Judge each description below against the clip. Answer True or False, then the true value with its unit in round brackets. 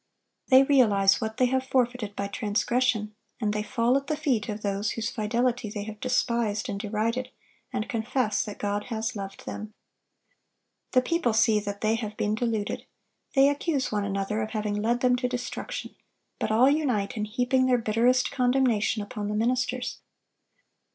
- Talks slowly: False (170 wpm)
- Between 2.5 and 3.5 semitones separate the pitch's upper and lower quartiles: True (3.1 semitones)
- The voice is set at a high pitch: True (225 Hz)